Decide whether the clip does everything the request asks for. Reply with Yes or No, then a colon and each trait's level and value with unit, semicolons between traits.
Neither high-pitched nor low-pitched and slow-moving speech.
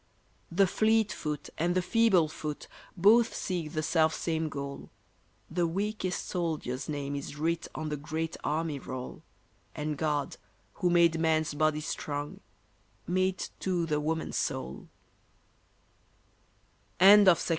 Yes: medium, 160 Hz; slow, 125 wpm